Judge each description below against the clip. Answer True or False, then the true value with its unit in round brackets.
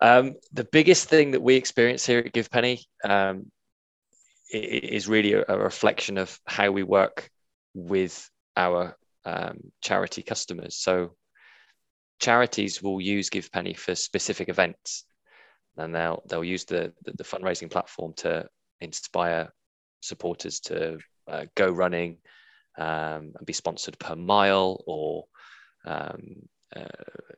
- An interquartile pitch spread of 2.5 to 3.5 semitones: False (5.1 semitones)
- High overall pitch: False (95 Hz)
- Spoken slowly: True (125 wpm)